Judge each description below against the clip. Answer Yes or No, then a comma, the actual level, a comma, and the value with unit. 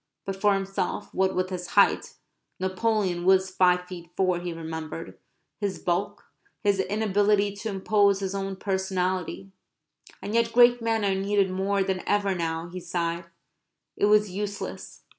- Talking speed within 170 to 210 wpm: No, average, 150 wpm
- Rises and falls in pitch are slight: Yes, narrow, 2.0 semitones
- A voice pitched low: No, high, 190 Hz